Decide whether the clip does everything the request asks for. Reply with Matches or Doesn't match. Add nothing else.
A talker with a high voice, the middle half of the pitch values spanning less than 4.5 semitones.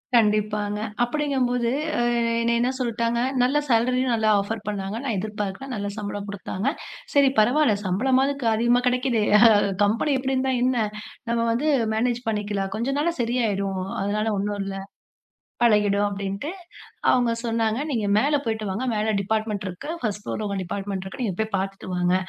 Matches